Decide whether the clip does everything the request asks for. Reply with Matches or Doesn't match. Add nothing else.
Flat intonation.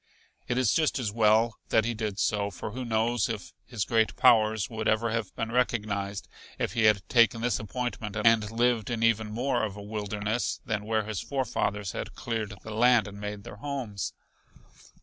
Matches